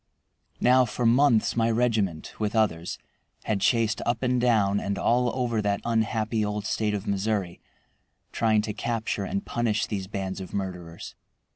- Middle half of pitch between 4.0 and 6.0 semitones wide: No, average, 2.8 semitones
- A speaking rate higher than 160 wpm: No, average, 155 wpm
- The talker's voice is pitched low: Yes, low, 110 Hz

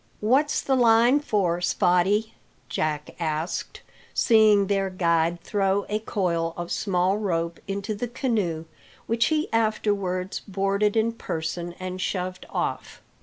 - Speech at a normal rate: No, slow, 125 wpm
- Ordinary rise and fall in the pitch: Yes, average, 3.8 semitones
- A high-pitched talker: Yes, high, 195 Hz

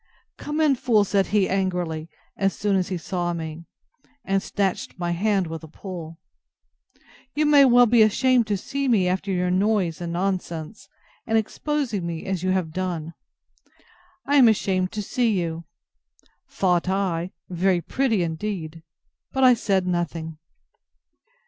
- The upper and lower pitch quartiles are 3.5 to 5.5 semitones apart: Yes, average, 3.8 semitones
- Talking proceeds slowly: No, average, 145 wpm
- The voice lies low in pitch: No, high, 190 Hz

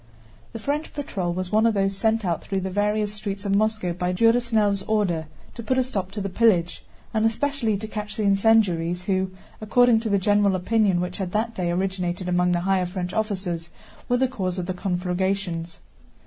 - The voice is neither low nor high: No, high, 195 Hz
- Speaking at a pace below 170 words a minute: No, average, 195 wpm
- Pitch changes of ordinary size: Yes, average, 3.3 semitones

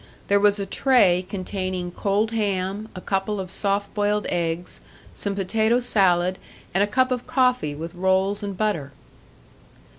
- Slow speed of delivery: No, average, 150 wpm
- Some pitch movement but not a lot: No, narrow, 2.3 semitones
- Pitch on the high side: Yes, high, 200 Hz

